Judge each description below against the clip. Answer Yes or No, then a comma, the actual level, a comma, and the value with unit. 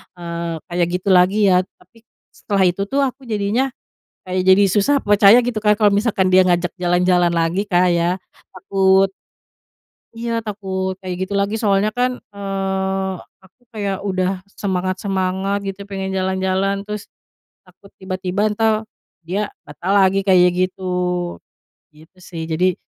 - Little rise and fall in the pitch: Yes, narrow, 1.9 semitones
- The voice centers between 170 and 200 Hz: Yes, high, 190 Hz